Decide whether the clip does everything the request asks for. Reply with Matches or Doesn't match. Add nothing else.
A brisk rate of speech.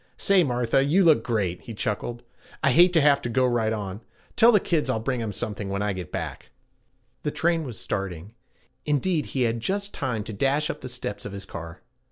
Matches